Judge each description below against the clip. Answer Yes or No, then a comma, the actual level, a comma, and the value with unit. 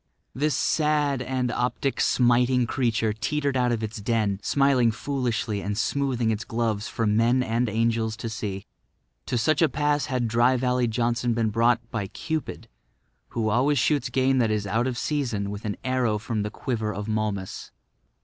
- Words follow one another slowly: No, average, 170 wpm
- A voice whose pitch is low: Yes, low, 120 Hz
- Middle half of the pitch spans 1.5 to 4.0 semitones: Yes, average, 2.9 semitones